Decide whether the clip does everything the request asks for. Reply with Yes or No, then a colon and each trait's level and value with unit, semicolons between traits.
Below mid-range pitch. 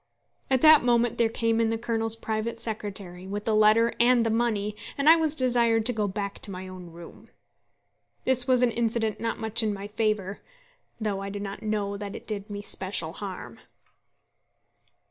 No: high, 220 Hz